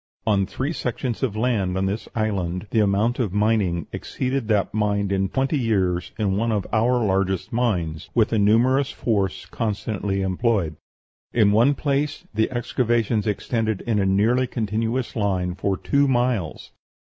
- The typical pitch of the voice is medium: No, low, 110 Hz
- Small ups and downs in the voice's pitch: No, average, 3.6 semitones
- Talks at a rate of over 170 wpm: No, average, 155 wpm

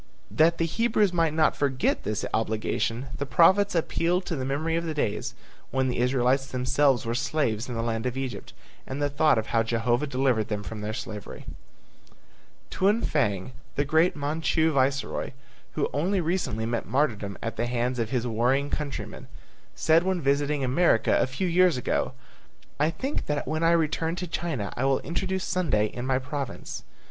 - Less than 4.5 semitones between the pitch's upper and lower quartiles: No, average, 5.2 semitones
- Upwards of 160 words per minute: Yes, average, 175 wpm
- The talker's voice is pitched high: No, medium, 140 Hz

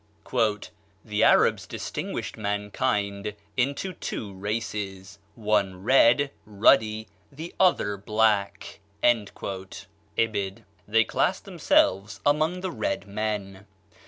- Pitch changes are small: No, average, 3.4 semitones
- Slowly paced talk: Yes, slow, 90 wpm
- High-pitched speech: No, low, 105 Hz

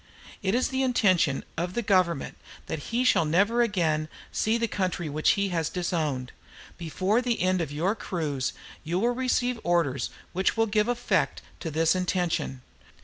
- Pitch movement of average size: No, wide, 5.8 semitones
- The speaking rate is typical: Yes, average, 165 wpm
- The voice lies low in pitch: No, medium, 185 Hz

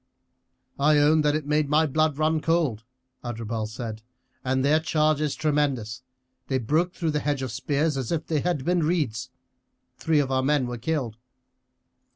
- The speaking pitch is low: No, medium, 145 Hz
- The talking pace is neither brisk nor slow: Yes, average, 175 wpm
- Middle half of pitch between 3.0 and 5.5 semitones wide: Yes, average, 3.3 semitones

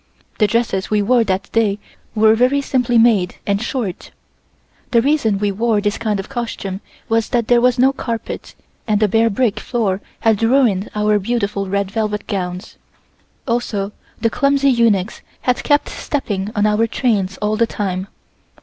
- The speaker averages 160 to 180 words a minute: Yes, average, 165 wpm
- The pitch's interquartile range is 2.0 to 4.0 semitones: Yes, average, 3.0 semitones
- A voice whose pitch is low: No, high, 220 Hz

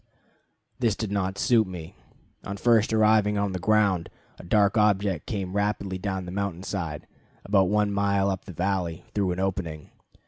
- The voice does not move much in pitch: Yes, narrow, 1.9 semitones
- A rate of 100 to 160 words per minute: No, average, 170 wpm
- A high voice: No, low, 100 Hz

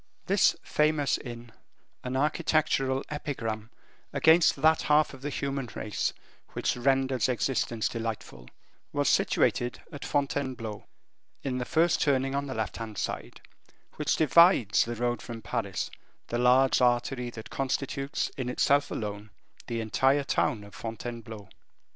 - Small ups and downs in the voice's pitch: No, average, 3.5 semitones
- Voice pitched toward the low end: Yes, low, 125 Hz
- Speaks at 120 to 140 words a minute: Yes, slow, 135 wpm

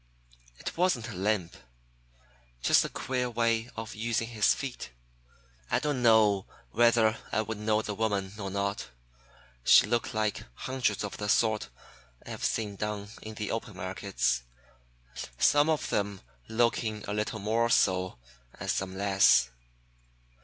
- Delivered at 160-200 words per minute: No, average, 145 wpm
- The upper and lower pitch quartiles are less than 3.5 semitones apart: Yes, narrow, 2.5 semitones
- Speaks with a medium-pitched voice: No, low, 110 Hz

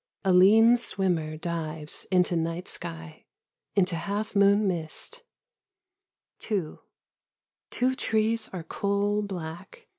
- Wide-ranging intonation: No, average, 4.0 semitones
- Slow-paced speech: Yes, slow, 100 wpm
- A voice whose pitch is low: No, high, 190 Hz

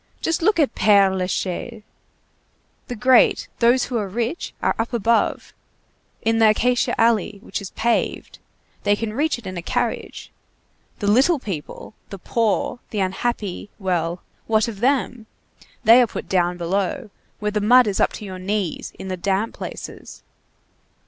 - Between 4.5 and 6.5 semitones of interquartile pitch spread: No, average, 3.8 semitones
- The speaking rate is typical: Yes, average, 160 wpm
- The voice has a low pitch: No, high, 215 Hz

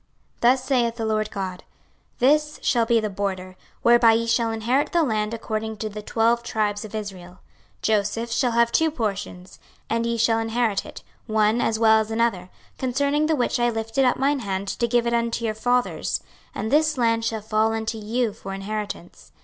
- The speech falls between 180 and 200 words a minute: Yes, average, 195 wpm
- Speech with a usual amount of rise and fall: No, narrow, 1.9 semitones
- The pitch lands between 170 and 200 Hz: No, high, 225 Hz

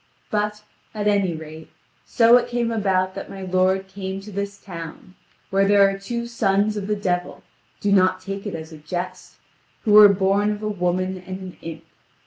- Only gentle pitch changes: Yes, narrow, 2.0 semitones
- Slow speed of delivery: No, average, 190 wpm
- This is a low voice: No, high, 195 Hz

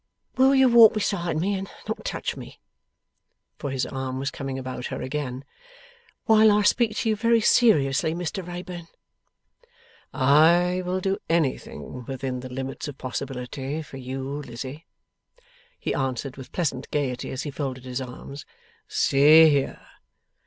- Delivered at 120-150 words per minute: Yes, average, 145 wpm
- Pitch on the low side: No, medium, 145 Hz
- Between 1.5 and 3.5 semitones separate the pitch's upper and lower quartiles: No, wide, 5.4 semitones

